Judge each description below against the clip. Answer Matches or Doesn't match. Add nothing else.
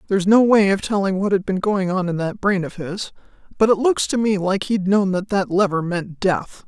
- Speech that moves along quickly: Matches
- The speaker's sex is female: Matches